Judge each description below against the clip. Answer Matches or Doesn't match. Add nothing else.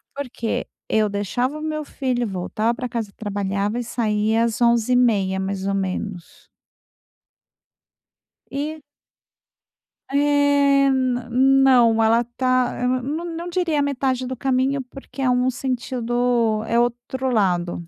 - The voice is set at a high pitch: Matches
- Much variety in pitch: Doesn't match